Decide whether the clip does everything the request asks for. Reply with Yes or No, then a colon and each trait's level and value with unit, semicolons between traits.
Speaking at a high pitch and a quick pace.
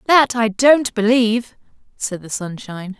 No: high, 225 Hz; average, 140 wpm